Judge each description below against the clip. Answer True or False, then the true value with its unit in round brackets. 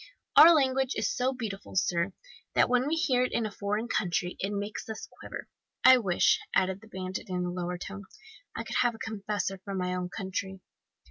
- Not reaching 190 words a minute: False (200 wpm)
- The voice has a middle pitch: False (200 Hz)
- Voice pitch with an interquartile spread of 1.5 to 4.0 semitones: False (4.6 semitones)